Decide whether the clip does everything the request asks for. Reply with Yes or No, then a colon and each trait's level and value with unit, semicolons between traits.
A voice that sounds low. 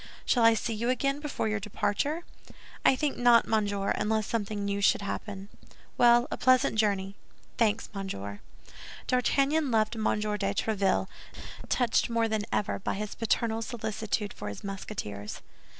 No: high, 215 Hz